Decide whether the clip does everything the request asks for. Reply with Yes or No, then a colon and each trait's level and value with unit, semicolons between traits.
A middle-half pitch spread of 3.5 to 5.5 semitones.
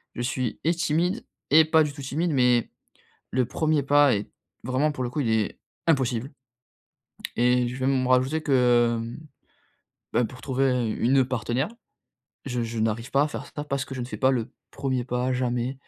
No: average, 2.7 semitones